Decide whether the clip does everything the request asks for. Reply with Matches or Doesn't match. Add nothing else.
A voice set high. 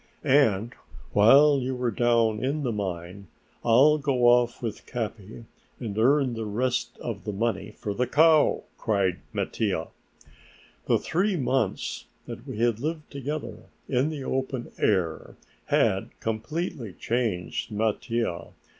Doesn't match